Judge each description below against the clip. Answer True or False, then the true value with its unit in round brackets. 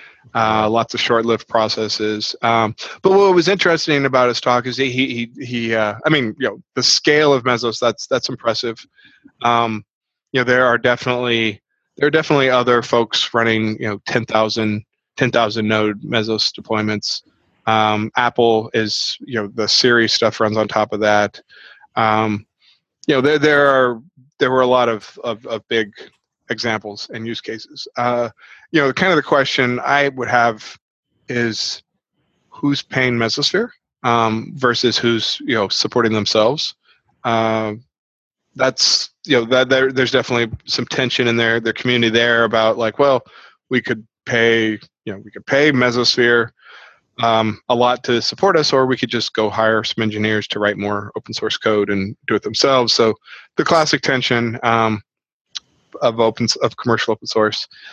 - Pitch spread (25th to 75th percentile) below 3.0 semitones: True (2.5 semitones)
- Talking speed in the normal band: True (170 wpm)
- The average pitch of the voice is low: True (115 Hz)